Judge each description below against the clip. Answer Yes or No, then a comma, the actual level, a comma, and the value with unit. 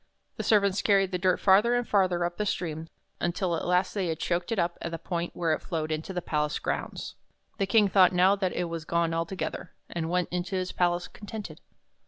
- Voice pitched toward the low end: No, medium, 180 Hz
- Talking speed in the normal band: No, fast, 225 wpm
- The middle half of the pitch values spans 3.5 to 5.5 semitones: No, narrow, 2.4 semitones